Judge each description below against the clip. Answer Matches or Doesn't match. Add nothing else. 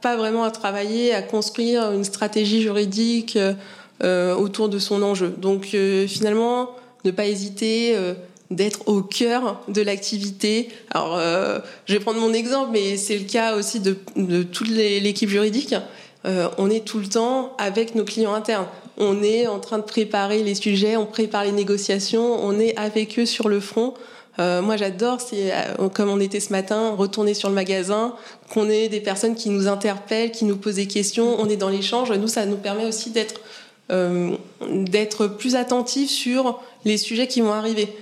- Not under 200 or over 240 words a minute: Doesn't match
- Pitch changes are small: Matches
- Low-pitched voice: Doesn't match